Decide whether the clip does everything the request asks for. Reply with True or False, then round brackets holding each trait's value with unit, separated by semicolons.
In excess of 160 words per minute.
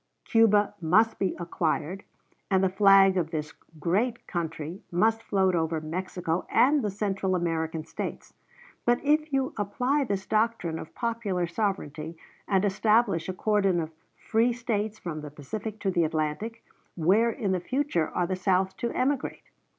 False (155 wpm)